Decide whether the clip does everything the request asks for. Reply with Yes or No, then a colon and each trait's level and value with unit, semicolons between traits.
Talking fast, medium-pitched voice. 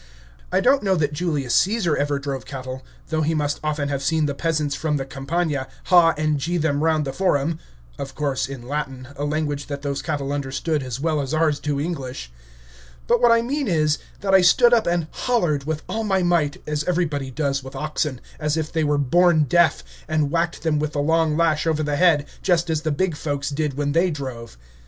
Yes: fast, 210 wpm; medium, 150 Hz